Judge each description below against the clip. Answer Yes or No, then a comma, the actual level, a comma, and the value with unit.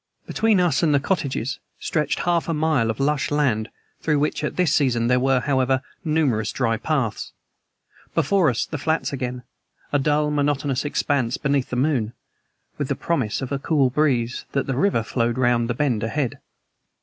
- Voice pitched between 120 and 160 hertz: Yes, medium, 140 Hz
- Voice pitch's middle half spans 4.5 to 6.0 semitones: No, average, 3.5 semitones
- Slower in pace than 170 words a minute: No, average, 175 wpm